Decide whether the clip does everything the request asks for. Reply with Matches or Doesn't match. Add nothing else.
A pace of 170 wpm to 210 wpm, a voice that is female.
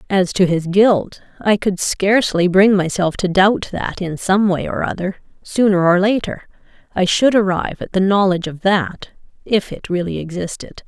Matches